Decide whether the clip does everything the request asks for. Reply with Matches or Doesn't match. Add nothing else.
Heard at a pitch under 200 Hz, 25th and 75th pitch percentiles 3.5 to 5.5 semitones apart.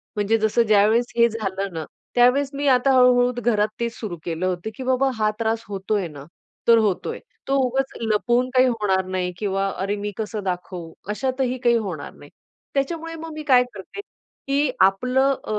Doesn't match